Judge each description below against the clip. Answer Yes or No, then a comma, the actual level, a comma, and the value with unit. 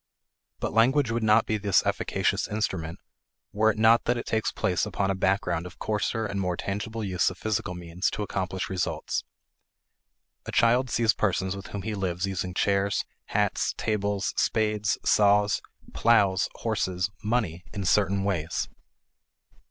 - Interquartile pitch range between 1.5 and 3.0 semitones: Yes, average, 2.7 semitones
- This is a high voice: No, low, 100 Hz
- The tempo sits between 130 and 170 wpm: Yes, average, 150 wpm